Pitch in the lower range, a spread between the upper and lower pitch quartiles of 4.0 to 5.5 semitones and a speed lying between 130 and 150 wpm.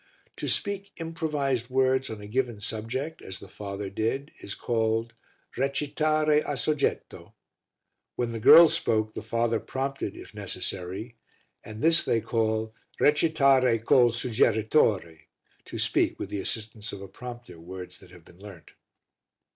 Yes: low, 115 Hz; average, 4.8 semitones; average, 140 wpm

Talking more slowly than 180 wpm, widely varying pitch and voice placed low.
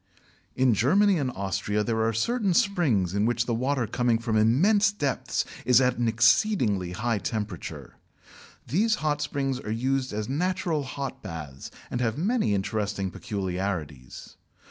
Yes: average, 145 wpm; wide, 5.7 semitones; low, 120 Hz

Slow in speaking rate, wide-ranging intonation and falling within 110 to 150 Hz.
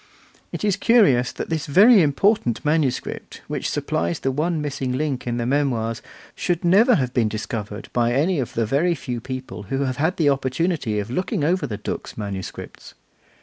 No: average, 175 wpm; wide, 5.7 semitones; low, 135 Hz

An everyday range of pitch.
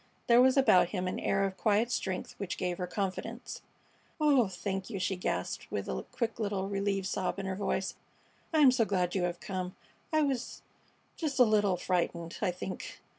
Yes: average, 3.9 semitones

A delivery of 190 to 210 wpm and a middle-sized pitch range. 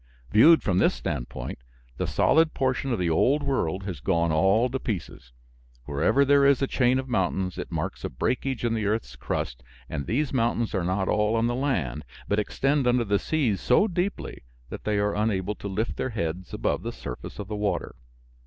No: average, 200 wpm; wide, 5.7 semitones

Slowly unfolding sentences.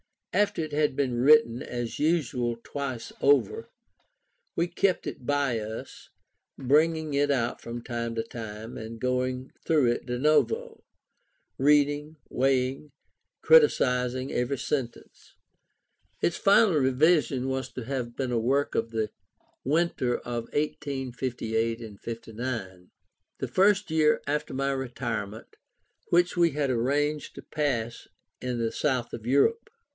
Yes: slow, 130 wpm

